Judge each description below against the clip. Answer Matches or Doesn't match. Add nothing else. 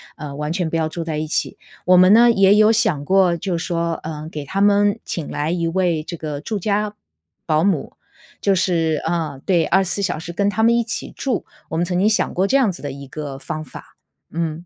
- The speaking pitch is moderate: Matches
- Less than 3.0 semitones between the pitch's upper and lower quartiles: Doesn't match